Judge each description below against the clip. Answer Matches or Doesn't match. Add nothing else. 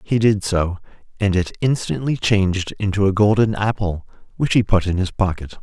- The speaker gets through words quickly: Doesn't match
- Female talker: Doesn't match